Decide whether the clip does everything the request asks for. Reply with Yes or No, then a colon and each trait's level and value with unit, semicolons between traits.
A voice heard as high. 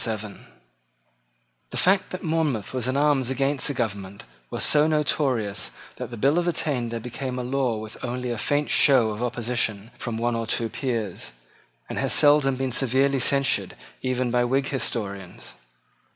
No: low, 125 Hz